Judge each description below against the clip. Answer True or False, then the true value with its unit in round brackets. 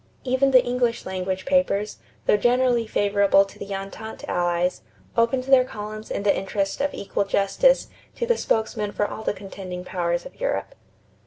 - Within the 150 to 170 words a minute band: True (165 wpm)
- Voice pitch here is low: False (210 Hz)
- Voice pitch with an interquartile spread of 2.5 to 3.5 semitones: False (4.3 semitones)